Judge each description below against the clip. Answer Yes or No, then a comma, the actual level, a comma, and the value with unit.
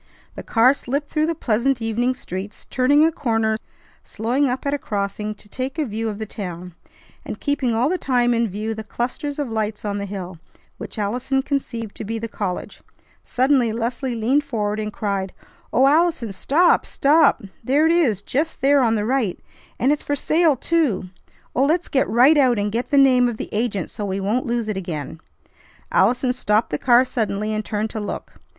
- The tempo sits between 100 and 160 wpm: No, average, 195 wpm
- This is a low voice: No, high, 235 Hz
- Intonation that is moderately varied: Yes, average, 4.5 semitones